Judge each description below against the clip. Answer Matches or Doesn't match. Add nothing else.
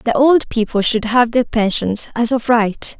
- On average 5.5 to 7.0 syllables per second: Doesn't match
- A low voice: Doesn't match